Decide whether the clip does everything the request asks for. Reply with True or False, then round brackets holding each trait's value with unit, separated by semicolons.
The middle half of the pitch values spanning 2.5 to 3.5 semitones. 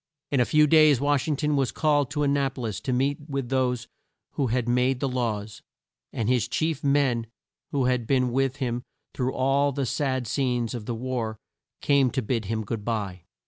True (2.9 semitones)